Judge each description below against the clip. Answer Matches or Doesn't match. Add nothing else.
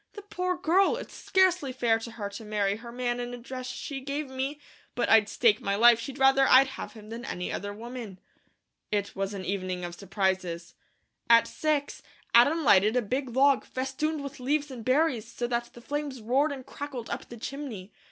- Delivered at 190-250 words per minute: Matches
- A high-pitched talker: Matches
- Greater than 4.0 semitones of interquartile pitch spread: Matches